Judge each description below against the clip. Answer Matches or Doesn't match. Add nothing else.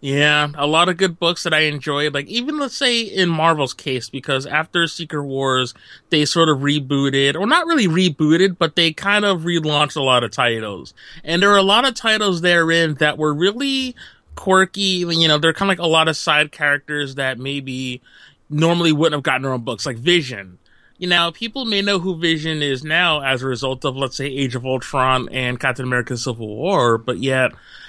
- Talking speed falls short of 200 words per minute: Doesn't match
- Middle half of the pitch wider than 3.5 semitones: Matches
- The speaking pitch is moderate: Matches